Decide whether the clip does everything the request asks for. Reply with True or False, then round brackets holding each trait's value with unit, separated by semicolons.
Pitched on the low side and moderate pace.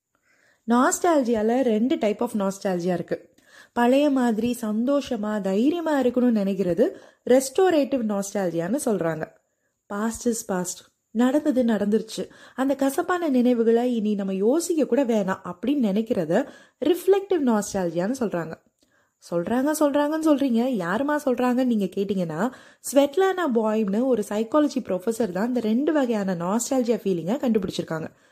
False (240 Hz; 100 wpm)